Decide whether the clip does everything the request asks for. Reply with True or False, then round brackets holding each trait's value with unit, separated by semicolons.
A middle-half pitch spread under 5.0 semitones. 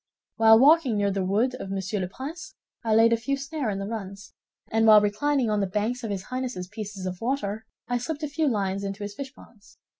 True (4.3 semitones)